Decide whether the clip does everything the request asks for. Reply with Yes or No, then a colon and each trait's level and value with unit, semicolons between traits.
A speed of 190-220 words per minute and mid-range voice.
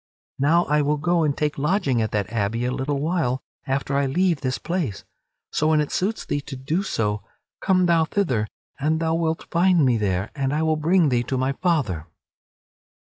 Yes: average, 195 wpm; medium, 145 Hz